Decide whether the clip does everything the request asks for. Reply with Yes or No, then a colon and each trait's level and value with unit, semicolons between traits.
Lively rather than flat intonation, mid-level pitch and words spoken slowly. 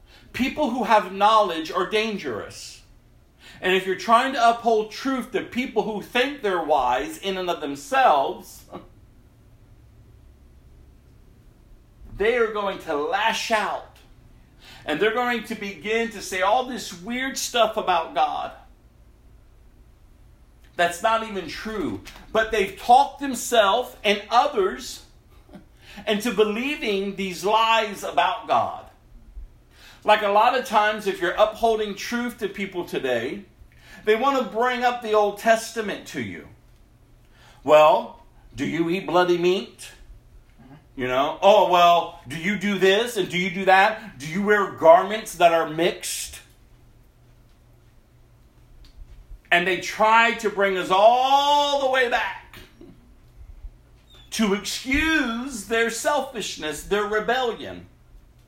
No: wide, 5.8 semitones; high, 205 Hz; slow, 125 wpm